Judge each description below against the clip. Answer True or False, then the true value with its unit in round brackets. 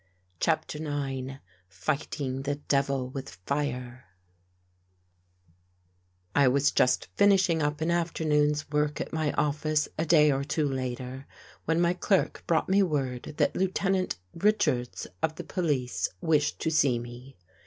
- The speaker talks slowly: True (130 wpm)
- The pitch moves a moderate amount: True (3.3 semitones)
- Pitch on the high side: False (145 Hz)